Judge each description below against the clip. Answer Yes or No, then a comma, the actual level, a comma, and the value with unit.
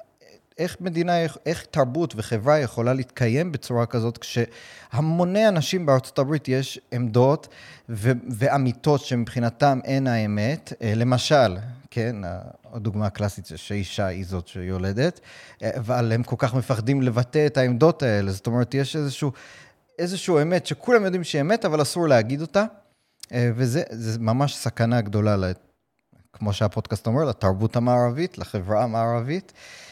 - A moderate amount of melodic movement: Yes, average, 4.5 semitones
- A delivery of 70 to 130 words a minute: Yes, average, 125 wpm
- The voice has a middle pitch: No, low, 125 Hz